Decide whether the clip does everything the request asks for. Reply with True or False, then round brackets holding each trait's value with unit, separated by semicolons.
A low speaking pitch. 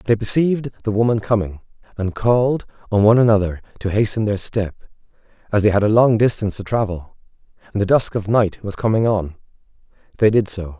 True (105 Hz)